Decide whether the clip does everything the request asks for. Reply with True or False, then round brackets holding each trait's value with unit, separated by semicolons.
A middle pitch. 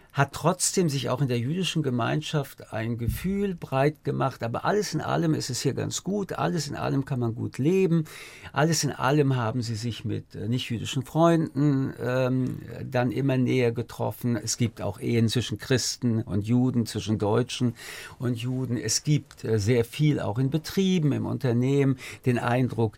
False (130 Hz)